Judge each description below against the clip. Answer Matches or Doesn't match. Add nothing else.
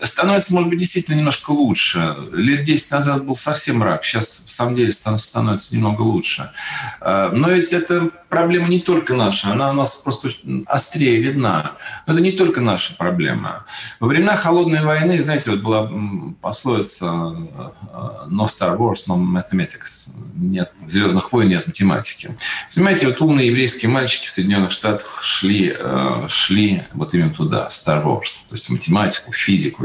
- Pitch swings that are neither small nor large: Doesn't match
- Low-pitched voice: Matches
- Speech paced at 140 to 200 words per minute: Matches